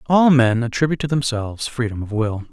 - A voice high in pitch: No, low, 125 Hz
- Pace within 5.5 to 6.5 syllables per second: Yes, 5.9 syllables/s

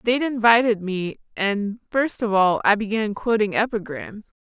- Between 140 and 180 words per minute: Yes, average, 150 wpm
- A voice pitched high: Yes, high, 215 Hz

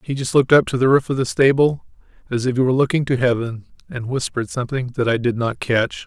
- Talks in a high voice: No, low, 125 Hz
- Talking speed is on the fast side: Yes, fast, 245 wpm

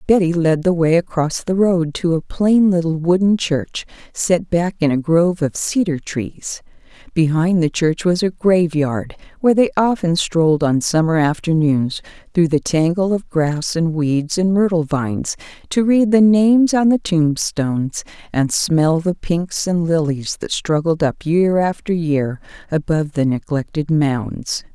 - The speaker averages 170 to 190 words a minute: No, average, 160 wpm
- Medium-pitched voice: Yes, medium, 170 Hz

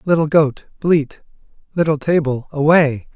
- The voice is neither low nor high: Yes, medium, 150 Hz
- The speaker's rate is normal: No, slow, 115 wpm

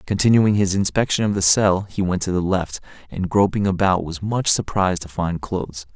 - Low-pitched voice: Yes, very low, 95 Hz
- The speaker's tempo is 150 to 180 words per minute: No, average, 200 wpm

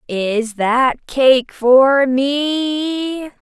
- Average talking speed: No, slow, 85 wpm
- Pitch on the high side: Yes, very high, 280 Hz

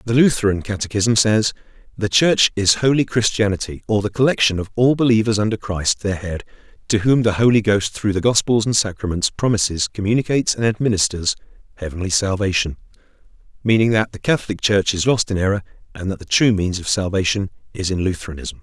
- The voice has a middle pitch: No, low, 105 Hz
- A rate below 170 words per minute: No, average, 175 wpm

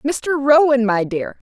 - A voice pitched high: Yes, very high, 260 Hz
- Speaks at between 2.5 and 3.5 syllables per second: No, 3.7 syllables/s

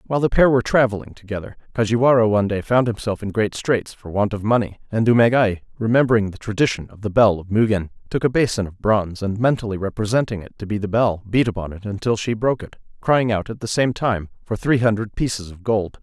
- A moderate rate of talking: No, fast, 220 wpm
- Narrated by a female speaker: No, male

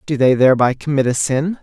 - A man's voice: Yes, male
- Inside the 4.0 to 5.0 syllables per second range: No, 6.0 syllables/s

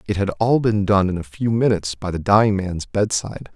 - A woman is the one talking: No, male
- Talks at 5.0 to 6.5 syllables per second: Yes, 5.5 syllables/s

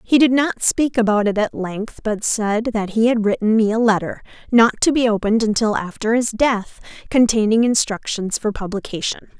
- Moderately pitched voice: No, high, 220 Hz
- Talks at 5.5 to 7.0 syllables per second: No, 5.1 syllables/s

